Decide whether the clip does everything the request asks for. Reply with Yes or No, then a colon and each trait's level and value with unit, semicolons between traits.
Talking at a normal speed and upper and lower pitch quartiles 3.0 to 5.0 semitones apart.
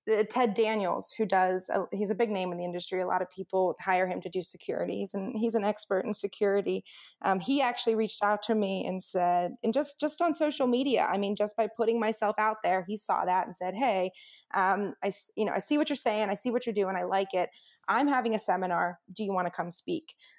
No: fast, 235 wpm; average, 3.5 semitones